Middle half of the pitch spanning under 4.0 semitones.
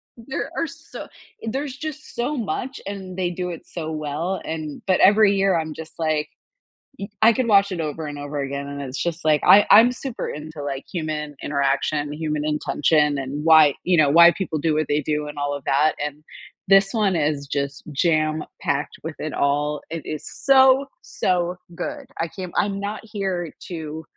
No: average, 4.8 semitones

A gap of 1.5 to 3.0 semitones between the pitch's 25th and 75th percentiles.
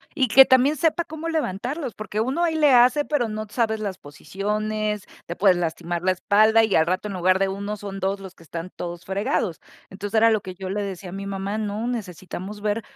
No: average, 3.4 semitones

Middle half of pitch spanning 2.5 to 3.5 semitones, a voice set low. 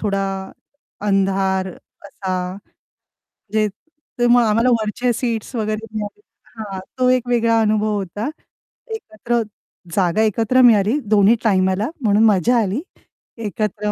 No: average, 2.9 semitones; high, 215 Hz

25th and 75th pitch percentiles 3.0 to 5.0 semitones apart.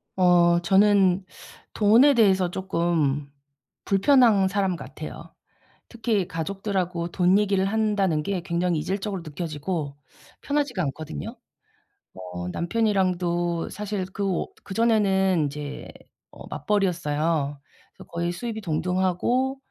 Yes: average, 3.3 semitones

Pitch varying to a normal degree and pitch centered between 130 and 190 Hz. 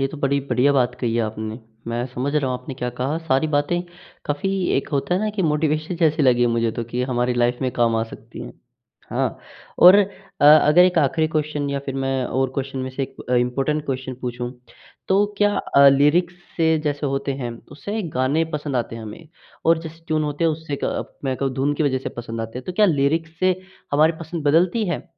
Yes: average, 4.0 semitones; medium, 140 Hz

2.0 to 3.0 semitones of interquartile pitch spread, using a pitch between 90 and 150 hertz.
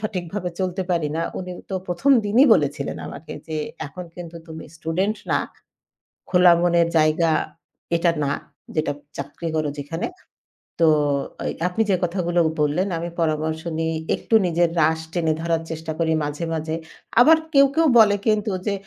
No: narrow, 2.6 semitones; medium, 170 Hz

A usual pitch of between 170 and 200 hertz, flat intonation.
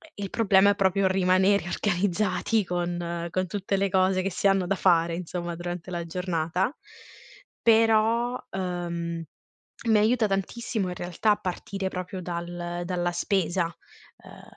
Yes: medium, 185 Hz; narrow, 2.3 semitones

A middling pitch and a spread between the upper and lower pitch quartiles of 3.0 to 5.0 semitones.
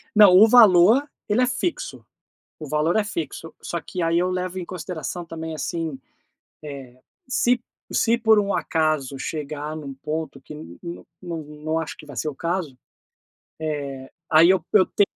Yes: medium, 165 Hz; average, 3.7 semitones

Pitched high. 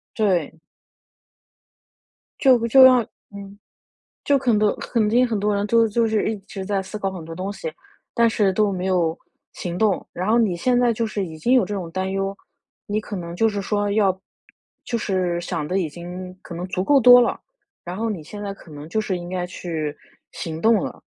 Yes: high, 200 Hz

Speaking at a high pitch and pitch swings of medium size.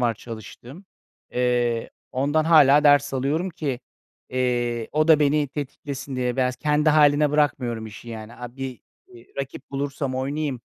No: low, 135 Hz; average, 3.3 semitones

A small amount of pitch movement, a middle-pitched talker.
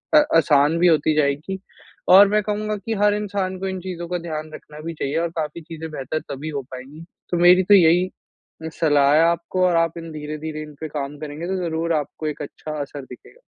No: average, 3.2 semitones; medium, 160 Hz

